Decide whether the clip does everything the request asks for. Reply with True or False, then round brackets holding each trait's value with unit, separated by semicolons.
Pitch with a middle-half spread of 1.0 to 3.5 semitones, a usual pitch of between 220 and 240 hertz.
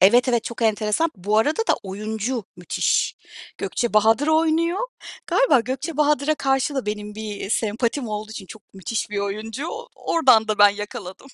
False (4.4 semitones; 225 Hz)